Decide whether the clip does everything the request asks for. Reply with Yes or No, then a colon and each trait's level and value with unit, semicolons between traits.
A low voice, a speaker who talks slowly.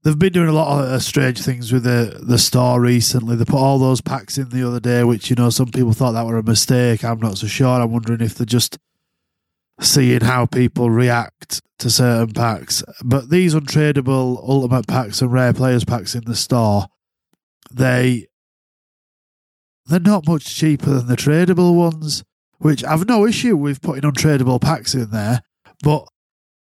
No: low, 125 Hz; average, 180 wpm